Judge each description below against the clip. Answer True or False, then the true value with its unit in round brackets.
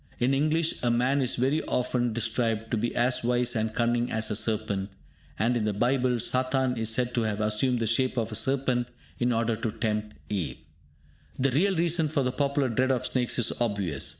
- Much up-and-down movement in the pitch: False (2.6 semitones)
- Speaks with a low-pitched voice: True (120 Hz)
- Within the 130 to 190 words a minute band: False (205 wpm)